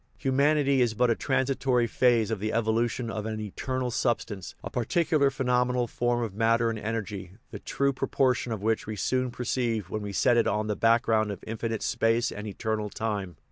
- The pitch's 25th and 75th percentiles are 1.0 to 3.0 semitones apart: Yes, narrow, 2.6 semitones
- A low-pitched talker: Yes, low, 115 Hz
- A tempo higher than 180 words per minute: Yes, average, 190 wpm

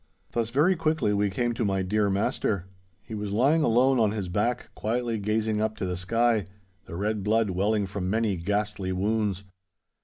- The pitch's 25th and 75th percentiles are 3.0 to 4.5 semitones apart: No, narrow, 2.6 semitones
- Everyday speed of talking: Yes, average, 180 wpm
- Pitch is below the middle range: Yes, low, 105 Hz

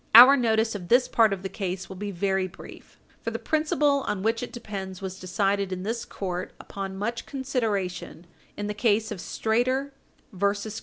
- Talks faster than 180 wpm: Yes, average, 190 wpm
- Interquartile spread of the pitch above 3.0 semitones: Yes, average, 3.5 semitones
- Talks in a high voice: Yes, high, 205 Hz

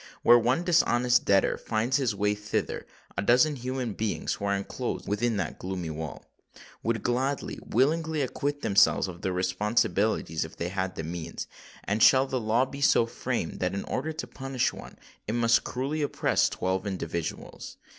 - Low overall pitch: Yes, low, 110 Hz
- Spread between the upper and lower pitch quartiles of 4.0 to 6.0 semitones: Yes, wide, 5.5 semitones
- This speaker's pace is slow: No, average, 165 wpm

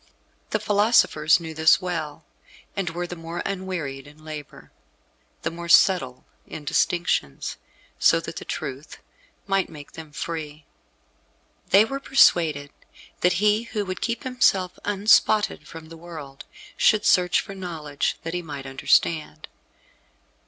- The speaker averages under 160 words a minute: Yes, slow, 135 wpm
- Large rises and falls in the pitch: No, average, 4.1 semitones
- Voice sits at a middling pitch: Yes, medium, 170 Hz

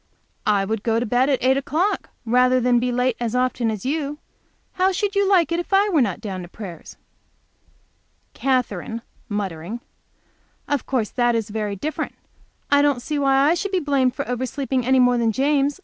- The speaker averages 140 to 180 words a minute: No, average, 190 wpm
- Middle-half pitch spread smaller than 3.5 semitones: No, average, 4.1 semitones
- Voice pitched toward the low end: No, very high, 255 Hz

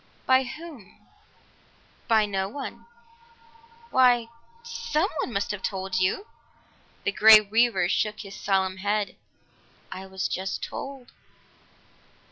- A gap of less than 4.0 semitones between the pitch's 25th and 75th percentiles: No, average, 5.2 semitones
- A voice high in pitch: Yes, high, 215 Hz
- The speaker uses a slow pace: Yes, slow, 105 wpm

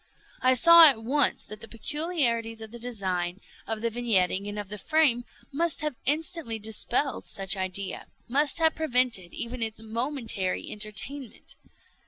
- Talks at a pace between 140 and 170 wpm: Yes, average, 145 wpm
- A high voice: Yes, high, 230 Hz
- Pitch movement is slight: No, average, 5.2 semitones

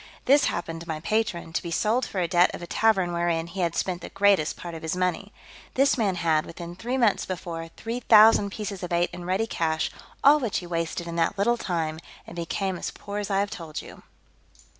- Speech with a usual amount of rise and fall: Yes, average, 3.5 semitones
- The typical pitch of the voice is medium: Yes, medium, 180 Hz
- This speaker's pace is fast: Yes, fast, 225 wpm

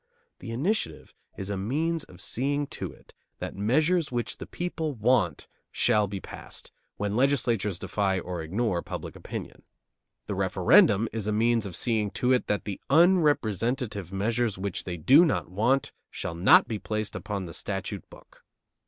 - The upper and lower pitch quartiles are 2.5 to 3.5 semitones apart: No, wide, 5.4 semitones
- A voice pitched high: No, low, 110 Hz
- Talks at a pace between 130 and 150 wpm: No, average, 160 wpm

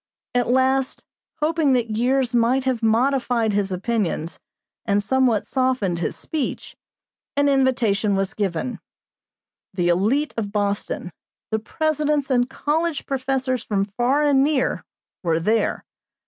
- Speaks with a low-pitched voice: No, high, 245 Hz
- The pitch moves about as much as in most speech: Yes, average, 4.6 semitones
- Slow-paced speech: Yes, slow, 125 wpm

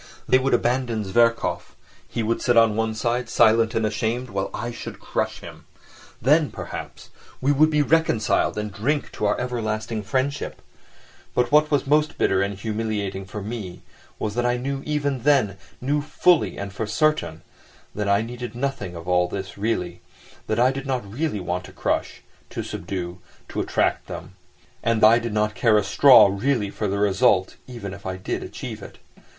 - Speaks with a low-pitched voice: Yes, low, 115 Hz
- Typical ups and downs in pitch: Yes, average, 4.4 semitones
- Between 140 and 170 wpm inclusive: No, average, 180 wpm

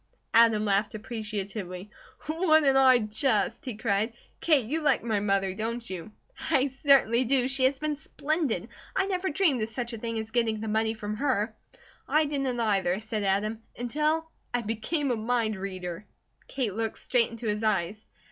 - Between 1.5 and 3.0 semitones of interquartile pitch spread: No, average, 4.1 semitones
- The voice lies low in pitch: No, high, 225 Hz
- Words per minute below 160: No, average, 170 wpm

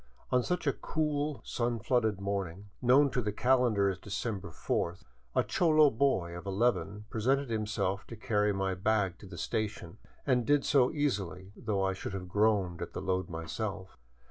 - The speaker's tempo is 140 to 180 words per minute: Yes, average, 170 wpm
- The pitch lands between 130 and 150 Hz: No, low, 105 Hz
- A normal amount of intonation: Yes, average, 4.5 semitones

